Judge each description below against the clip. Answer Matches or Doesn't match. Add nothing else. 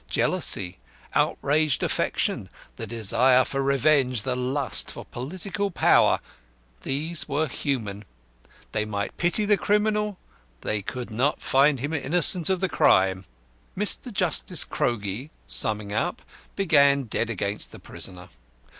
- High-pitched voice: Doesn't match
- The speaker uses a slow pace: Matches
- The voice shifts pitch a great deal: Matches